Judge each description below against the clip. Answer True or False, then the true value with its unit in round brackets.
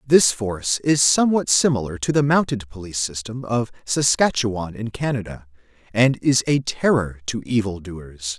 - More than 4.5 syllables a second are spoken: True (4.8 syllables/s)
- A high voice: False (115 Hz)